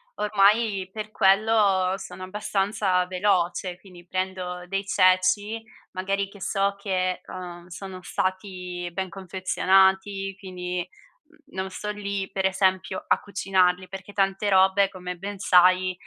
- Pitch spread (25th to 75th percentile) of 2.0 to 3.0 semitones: No, narrow, 1.3 semitones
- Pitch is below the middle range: No, high, 190 Hz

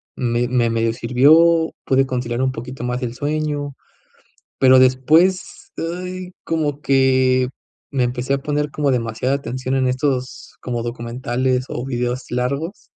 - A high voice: No, low, 130 Hz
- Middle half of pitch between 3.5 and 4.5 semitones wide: No, average, 2.7 semitones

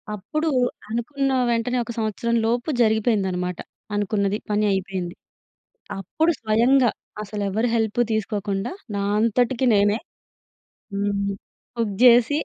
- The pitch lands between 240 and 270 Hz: No, high, 220 Hz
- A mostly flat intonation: No, average, 3.0 semitones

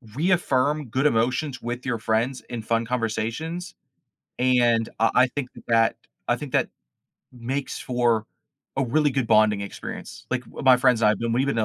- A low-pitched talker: Yes, low, 125 Hz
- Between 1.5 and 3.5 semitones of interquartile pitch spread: Yes, average, 2.8 semitones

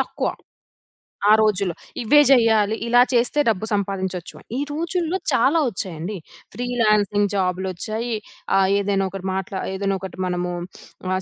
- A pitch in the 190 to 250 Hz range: Yes, high, 205 Hz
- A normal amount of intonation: Yes, average, 3.9 semitones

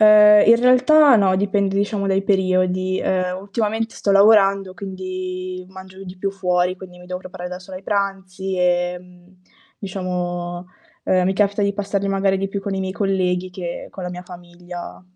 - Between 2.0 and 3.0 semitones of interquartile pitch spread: No, narrow, 1.6 semitones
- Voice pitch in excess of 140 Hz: Yes, high, 190 Hz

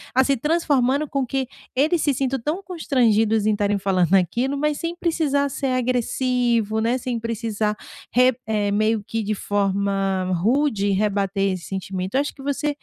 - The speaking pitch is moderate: No, high, 230 Hz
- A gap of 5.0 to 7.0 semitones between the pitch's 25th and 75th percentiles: Yes, average, 5.3 semitones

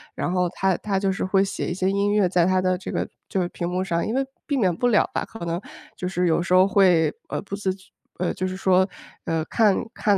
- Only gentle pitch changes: Yes, narrow, 1.8 semitones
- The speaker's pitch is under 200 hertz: Yes, medium, 185 Hz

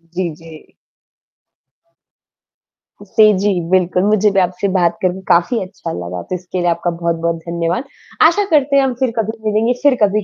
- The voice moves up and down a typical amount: Yes, average, 4.1 semitones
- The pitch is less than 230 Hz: Yes, medium, 185 Hz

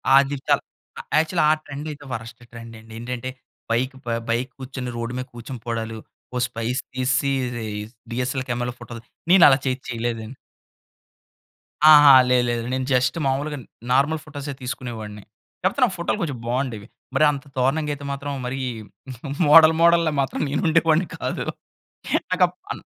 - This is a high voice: No, low, 130 Hz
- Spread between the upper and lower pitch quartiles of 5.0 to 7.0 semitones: No, average, 3.4 semitones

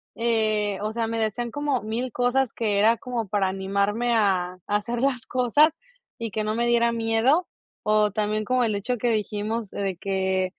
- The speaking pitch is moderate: No, high, 220 Hz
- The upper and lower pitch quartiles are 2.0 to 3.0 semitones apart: Yes, narrow, 2.5 semitones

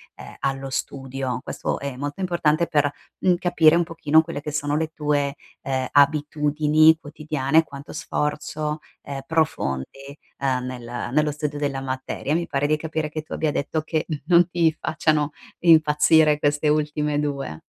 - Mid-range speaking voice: Yes, medium, 150 Hz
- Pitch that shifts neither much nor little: No, narrow, 2.0 semitones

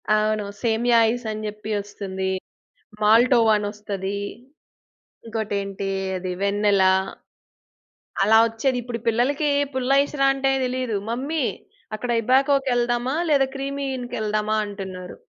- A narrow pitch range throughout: No, average, 3.8 semitones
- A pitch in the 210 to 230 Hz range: Yes, high, 225 Hz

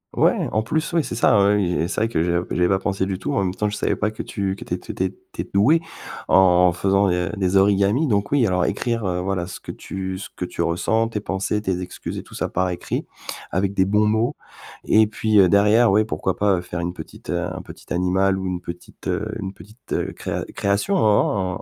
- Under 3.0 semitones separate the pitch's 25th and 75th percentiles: Yes, narrow, 2.5 semitones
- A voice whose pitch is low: Yes, very low, 95 Hz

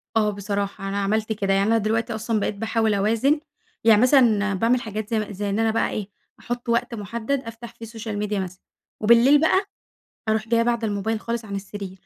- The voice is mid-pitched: No, high, 220 Hz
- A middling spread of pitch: No, narrow, 2.2 semitones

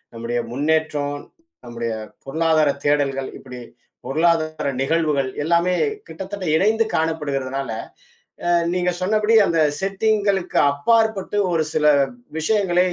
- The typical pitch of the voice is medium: Yes, medium, 160 Hz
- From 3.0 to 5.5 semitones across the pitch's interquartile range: Yes, average, 4.8 semitones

